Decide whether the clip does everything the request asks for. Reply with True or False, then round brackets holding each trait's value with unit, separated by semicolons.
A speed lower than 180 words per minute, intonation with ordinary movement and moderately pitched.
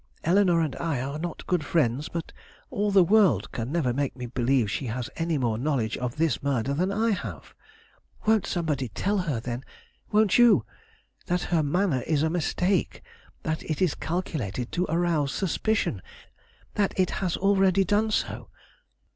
False (165 wpm; 6.2 semitones; 165 Hz)